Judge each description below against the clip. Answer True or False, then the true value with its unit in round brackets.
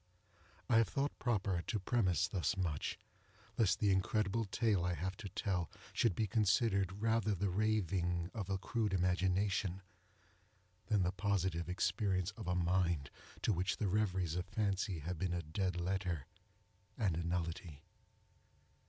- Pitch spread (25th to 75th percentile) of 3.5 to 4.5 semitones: False (2.8 semitones)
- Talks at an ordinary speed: True (150 wpm)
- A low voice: True (95 Hz)